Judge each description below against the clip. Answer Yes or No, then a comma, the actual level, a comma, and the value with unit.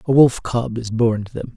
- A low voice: Yes, low, 115 Hz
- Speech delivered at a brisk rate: Yes, fast, 270 wpm